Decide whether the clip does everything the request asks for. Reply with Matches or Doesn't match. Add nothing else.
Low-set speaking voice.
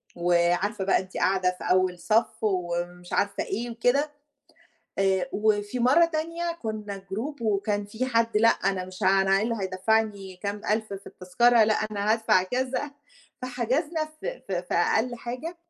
Doesn't match